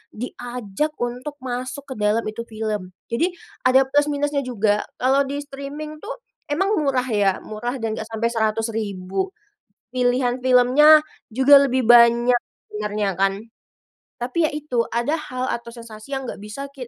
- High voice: Yes, high, 245 Hz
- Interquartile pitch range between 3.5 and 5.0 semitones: Yes, average, 4.2 semitones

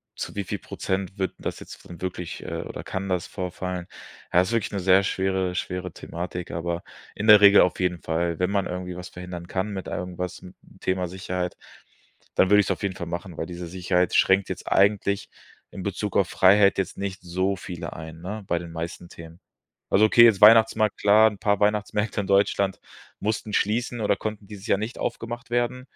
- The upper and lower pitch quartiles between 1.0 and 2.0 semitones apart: No, narrow, 2.4 semitones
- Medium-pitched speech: No, very low, 95 Hz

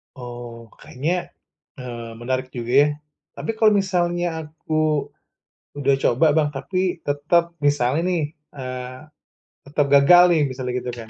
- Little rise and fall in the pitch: No, average, 4.5 semitones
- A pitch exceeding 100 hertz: Yes, medium, 140 Hz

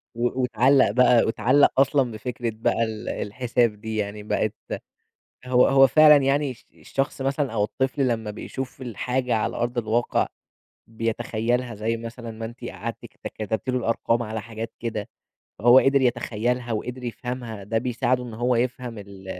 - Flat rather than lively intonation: Yes, narrow, 2.3 semitones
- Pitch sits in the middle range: No, low, 120 Hz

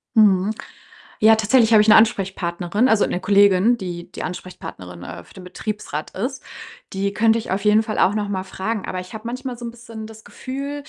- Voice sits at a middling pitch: No, high, 210 Hz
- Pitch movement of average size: Yes, average, 3.3 semitones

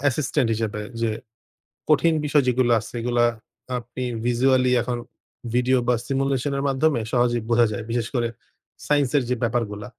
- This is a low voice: Yes, low, 125 Hz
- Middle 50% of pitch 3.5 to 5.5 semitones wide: No, narrow, 2.4 semitones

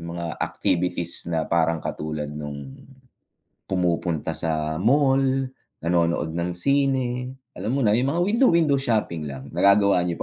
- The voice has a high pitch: No, very low, 90 Hz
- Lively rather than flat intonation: Yes, wide, 8.3 semitones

